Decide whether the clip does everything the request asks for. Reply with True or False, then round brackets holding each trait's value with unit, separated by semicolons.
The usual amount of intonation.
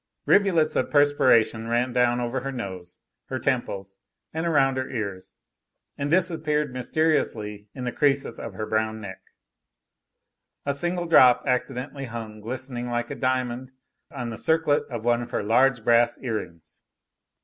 True (3.9 semitones)